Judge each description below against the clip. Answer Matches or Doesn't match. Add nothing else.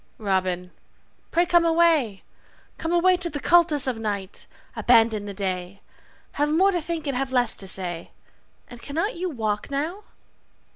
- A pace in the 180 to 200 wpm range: Doesn't match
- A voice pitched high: Matches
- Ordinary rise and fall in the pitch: Doesn't match